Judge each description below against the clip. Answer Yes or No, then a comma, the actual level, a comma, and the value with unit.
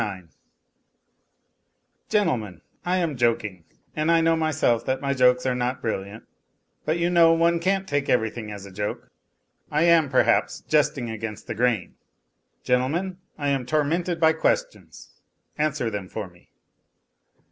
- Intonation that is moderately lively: No, wide, 6.7 semitones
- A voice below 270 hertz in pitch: Yes, low, 135 Hz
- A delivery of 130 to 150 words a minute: Yes, average, 145 wpm